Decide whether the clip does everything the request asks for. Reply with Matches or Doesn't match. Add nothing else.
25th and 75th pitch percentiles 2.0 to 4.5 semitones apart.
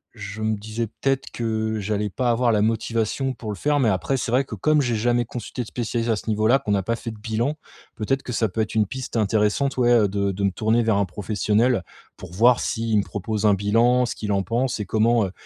Matches